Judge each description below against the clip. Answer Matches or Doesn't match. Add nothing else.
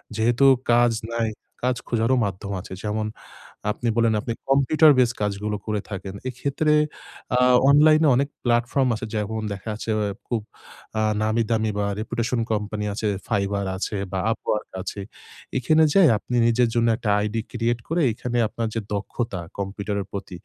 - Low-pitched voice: Matches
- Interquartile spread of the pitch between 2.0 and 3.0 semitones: Matches